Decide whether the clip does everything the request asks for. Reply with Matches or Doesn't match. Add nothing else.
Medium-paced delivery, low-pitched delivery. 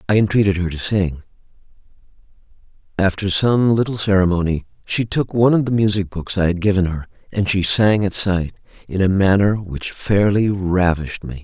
Matches